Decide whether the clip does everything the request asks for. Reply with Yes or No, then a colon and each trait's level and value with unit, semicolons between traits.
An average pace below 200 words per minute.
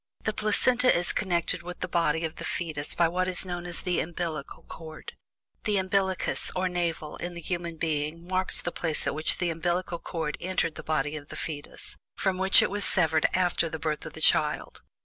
No: fast, 205 wpm